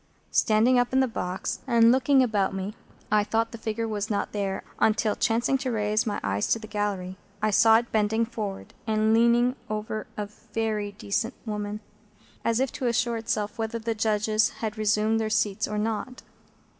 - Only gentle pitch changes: Yes, narrow, 1.7 semitones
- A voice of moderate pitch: No, high, 220 Hz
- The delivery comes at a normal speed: Yes, average, 180 wpm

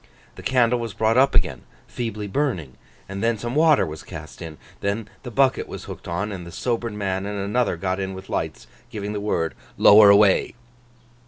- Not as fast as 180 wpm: No, average, 190 wpm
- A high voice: No, low, 105 Hz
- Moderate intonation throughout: Yes, average, 3.6 semitones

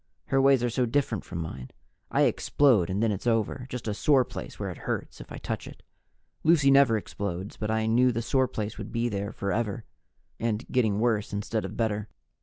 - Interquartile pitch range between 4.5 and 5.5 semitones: No, average, 3.4 semitones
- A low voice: Yes, low, 115 Hz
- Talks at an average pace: No, fast, 210 wpm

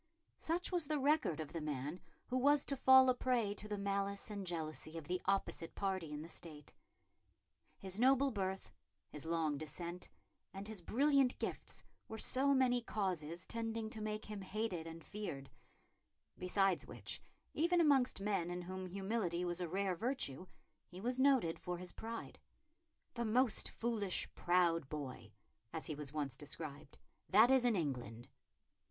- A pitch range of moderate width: No, wide, 6.0 semitones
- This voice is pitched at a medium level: No, high, 195 Hz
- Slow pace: No, average, 160 wpm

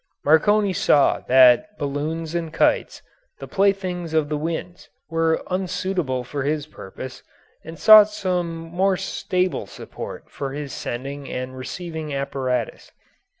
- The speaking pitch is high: No, medium, 160 Hz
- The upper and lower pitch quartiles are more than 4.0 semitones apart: Yes, average, 4.7 semitones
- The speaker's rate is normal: No, slow, 125 wpm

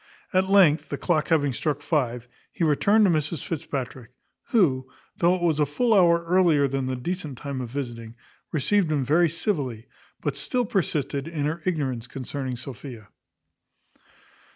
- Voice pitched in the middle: Yes, medium, 150 Hz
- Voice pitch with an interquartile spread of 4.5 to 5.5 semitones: Yes, average, 4.9 semitones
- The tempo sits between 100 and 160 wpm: Yes, average, 155 wpm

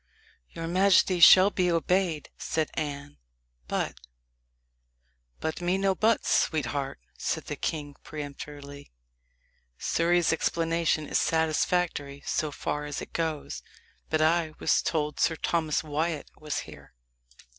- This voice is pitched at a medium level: Yes, medium, 155 Hz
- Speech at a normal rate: No, slow, 125 wpm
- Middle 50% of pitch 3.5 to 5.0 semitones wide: No, average, 2.8 semitones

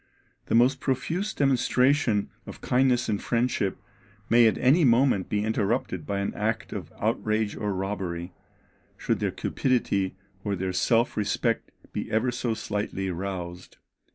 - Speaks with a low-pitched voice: Yes, low, 110 Hz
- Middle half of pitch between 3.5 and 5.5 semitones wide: Yes, average, 4.2 semitones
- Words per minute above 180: No, average, 140 wpm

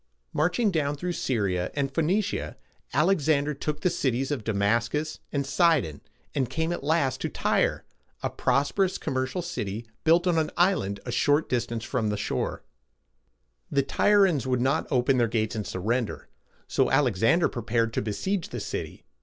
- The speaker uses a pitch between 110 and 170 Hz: Yes, low, 135 Hz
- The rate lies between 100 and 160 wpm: No, average, 170 wpm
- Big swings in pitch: Yes, wide, 5.7 semitones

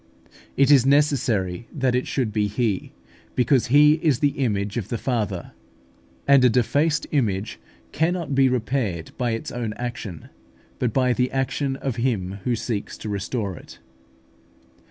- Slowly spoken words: No, average, 155 wpm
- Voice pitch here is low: Yes, low, 125 Hz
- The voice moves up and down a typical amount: Yes, average, 4.3 semitones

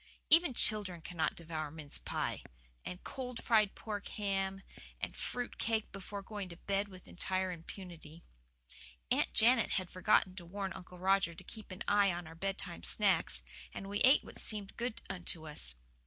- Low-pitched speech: No, high, 195 Hz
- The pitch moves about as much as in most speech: Yes, average, 3.3 semitones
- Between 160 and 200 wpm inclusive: Yes, average, 170 wpm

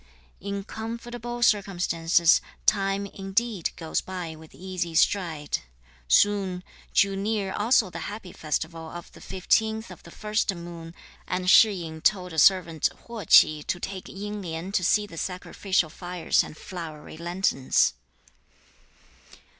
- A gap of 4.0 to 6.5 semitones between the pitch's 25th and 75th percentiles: No, average, 3.5 semitones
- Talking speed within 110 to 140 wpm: Yes, slow, 135 wpm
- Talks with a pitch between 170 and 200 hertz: Yes, medium, 185 Hz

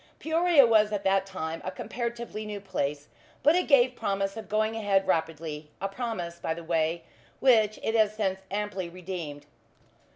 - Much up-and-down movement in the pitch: No, average, 4.6 semitones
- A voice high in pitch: Yes, high, 195 Hz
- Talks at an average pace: Yes, average, 165 wpm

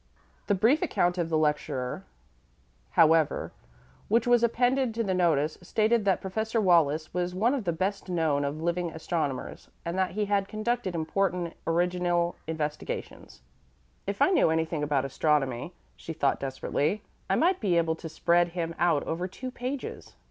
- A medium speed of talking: Yes, average, 160 wpm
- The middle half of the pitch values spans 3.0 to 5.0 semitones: Yes, average, 4.5 semitones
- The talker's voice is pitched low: No, medium, 175 Hz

